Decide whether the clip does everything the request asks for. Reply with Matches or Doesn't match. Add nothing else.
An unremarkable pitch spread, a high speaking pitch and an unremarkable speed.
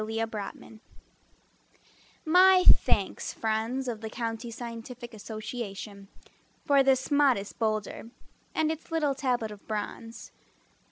Doesn't match